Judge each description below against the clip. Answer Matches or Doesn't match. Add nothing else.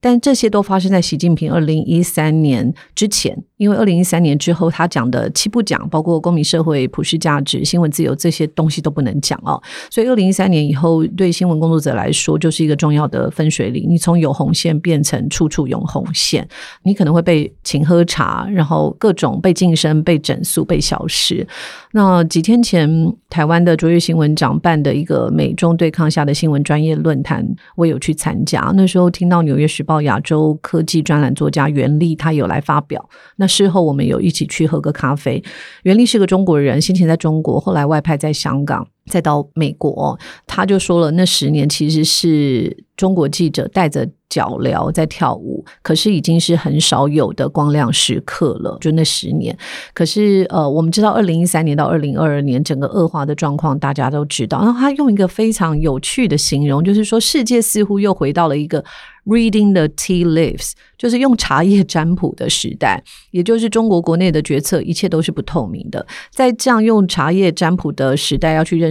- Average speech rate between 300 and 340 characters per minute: Matches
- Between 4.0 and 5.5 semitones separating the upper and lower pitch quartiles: Doesn't match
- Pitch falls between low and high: Matches